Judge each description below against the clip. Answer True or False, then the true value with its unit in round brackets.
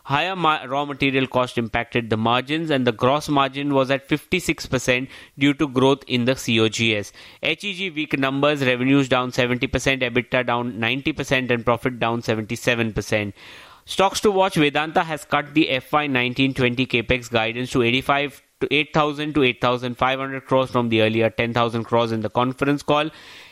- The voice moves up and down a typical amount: True (3.0 semitones)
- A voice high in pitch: False (130 Hz)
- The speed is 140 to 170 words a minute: True (155 wpm)